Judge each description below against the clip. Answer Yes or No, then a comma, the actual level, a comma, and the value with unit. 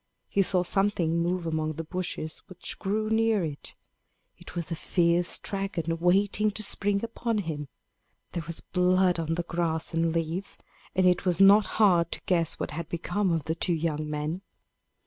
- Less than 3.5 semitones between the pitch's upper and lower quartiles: Yes, average, 3.0 semitones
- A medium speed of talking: Yes, average, 175 wpm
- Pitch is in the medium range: Yes, medium, 175 Hz